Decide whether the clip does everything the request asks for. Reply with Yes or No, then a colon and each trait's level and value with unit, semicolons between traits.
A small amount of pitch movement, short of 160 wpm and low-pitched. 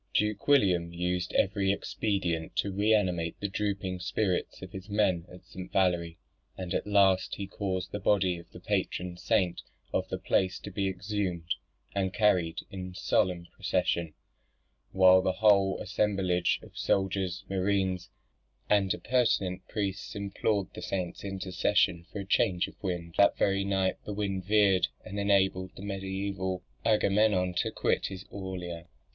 Yes: narrow, 1.8 semitones; average, 150 wpm; very low, 95 Hz